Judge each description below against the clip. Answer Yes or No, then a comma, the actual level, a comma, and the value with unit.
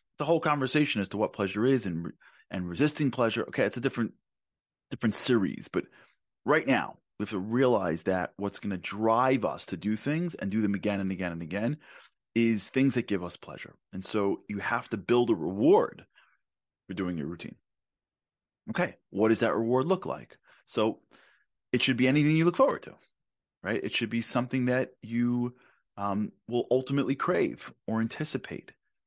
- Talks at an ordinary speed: Yes, average, 185 wpm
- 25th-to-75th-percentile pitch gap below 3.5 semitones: No, average, 4.7 semitones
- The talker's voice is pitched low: Yes, low, 115 Hz